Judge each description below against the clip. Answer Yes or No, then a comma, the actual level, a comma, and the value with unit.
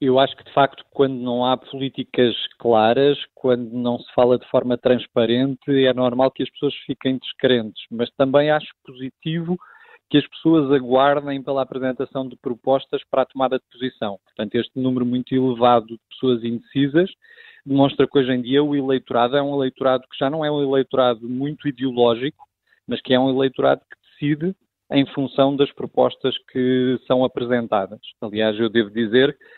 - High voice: No, low, 130 Hz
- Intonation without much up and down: Yes, narrow, 2.0 semitones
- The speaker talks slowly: No, average, 170 wpm